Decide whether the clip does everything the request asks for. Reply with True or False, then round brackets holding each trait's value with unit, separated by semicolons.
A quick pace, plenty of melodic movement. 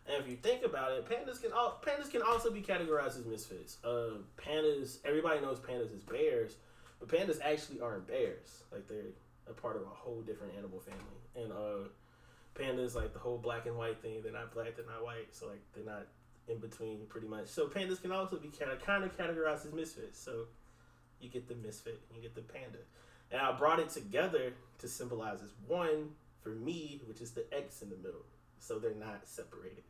True (215 wpm; 8.3 semitones)